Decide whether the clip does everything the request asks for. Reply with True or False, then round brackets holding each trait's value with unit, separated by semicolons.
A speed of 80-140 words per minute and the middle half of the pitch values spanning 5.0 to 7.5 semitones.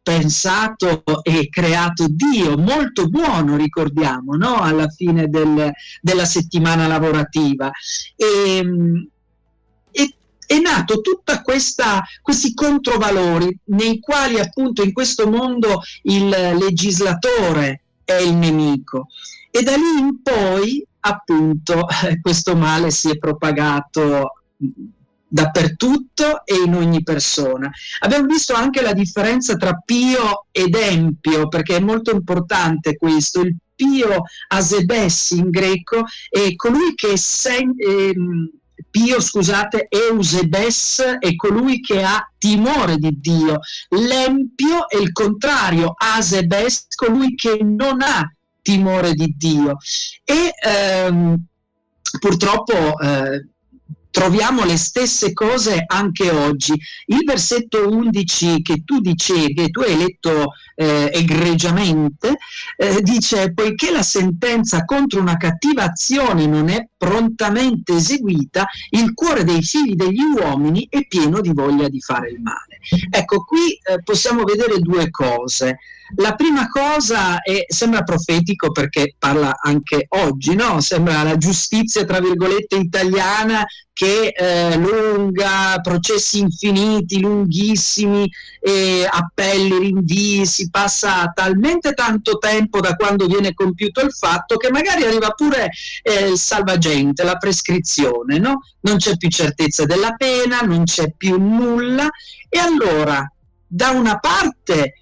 True (120 wpm; 5.3 semitones)